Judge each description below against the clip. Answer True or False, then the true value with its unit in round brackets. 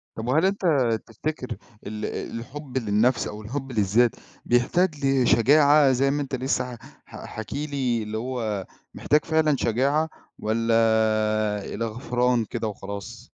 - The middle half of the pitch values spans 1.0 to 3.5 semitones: False (4.2 semitones)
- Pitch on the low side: True (120 Hz)